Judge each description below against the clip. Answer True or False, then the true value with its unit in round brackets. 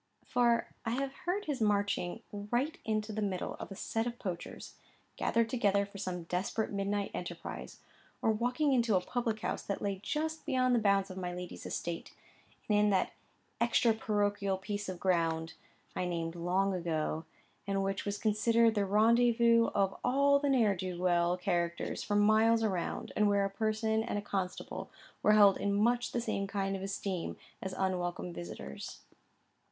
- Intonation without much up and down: False (3.6 semitones)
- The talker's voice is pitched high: True (205 Hz)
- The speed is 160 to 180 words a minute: True (175 wpm)